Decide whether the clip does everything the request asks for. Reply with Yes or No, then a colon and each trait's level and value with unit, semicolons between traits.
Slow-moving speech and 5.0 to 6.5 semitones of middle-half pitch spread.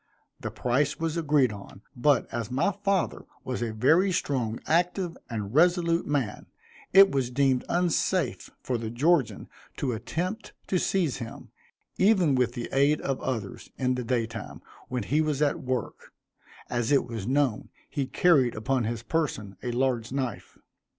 No: average, 160 wpm; average, 5.3 semitones